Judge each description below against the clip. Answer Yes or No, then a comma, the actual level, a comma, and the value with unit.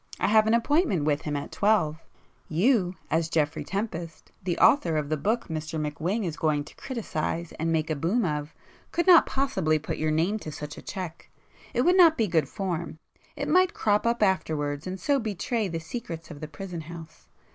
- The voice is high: No, medium, 170 Hz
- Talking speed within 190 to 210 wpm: Yes, average, 195 wpm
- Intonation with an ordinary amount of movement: No, wide, 5.8 semitones